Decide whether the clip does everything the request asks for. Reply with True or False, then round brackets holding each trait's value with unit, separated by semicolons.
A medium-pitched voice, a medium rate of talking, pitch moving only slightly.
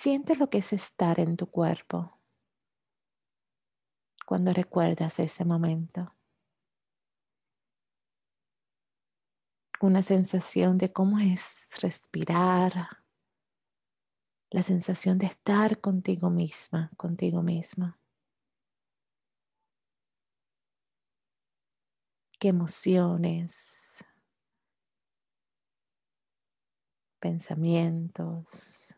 False (180 Hz; 60 wpm; 2.1 semitones)